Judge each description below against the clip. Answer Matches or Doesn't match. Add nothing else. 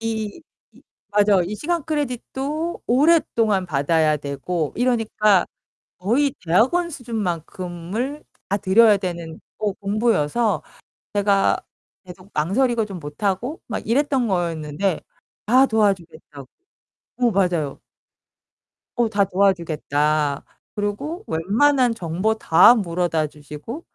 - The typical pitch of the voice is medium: Doesn't match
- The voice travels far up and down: Matches